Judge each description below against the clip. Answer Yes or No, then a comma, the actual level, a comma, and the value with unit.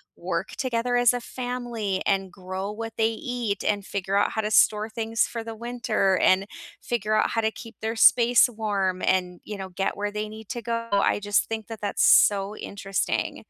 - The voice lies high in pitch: Yes, high, 215 Hz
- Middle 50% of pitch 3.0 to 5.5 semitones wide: No, narrow, 2.6 semitones